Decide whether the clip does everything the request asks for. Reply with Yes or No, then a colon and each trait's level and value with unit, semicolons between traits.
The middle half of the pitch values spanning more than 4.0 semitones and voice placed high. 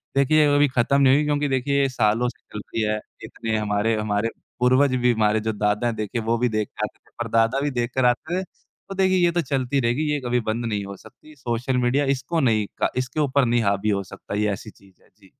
No: average, 4.4 semitones; low, 120 Hz